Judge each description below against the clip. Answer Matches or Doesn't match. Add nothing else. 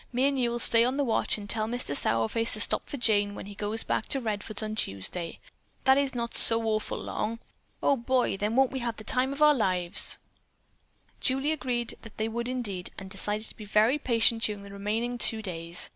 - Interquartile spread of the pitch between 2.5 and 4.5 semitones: Matches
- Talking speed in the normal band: Doesn't match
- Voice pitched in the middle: Doesn't match